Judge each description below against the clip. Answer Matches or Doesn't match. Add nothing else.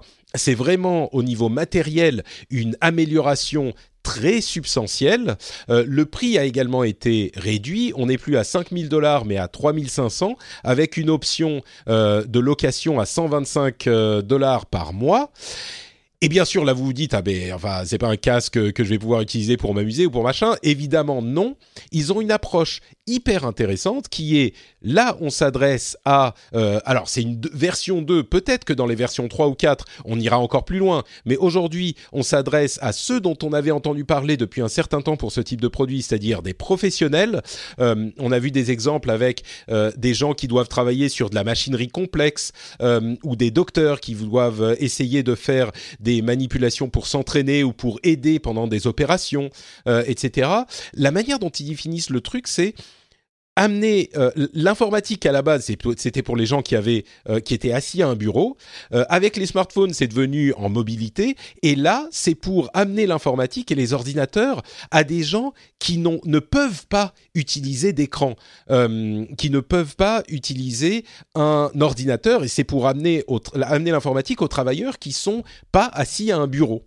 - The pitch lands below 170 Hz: Matches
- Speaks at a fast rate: Doesn't match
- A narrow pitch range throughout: Doesn't match